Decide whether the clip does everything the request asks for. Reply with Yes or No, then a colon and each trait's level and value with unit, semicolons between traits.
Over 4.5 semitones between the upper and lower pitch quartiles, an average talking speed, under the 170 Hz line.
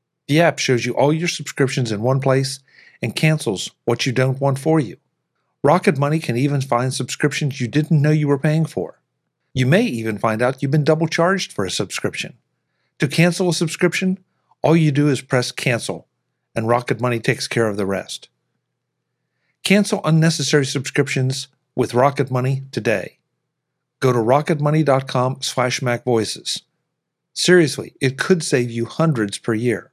No: average, 4.0 semitones; average, 160 wpm; medium, 140 Hz